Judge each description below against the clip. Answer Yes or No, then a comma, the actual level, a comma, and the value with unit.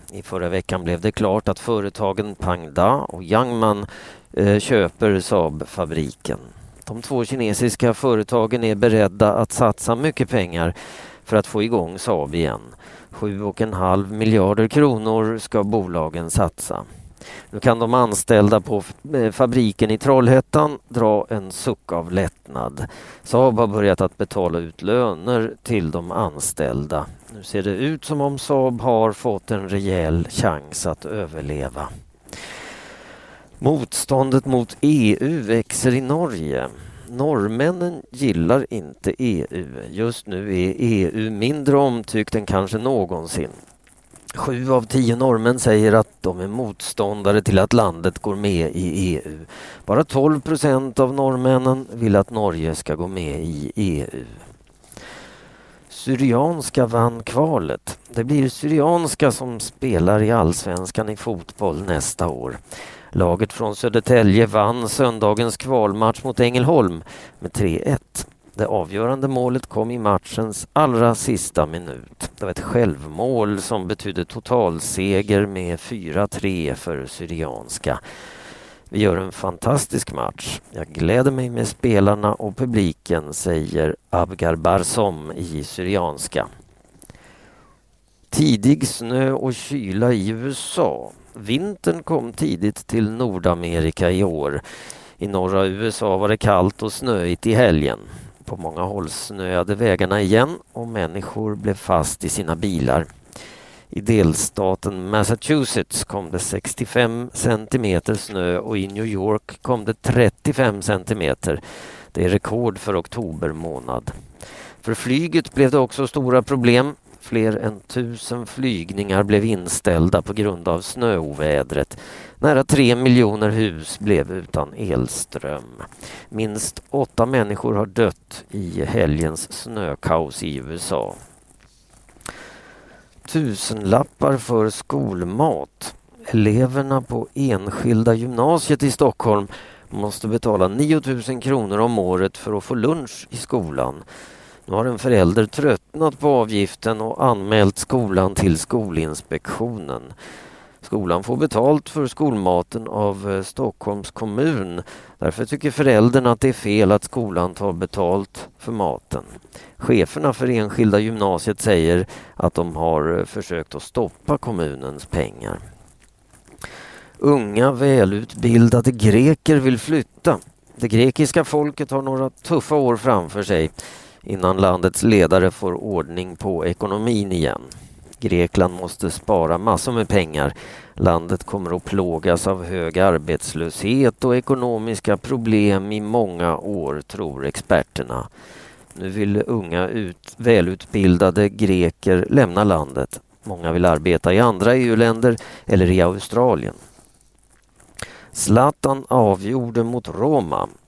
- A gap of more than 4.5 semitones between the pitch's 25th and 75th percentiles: Yes, average, 5.1 semitones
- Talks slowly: Yes, slow, 120 wpm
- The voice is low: Yes, low, 105 Hz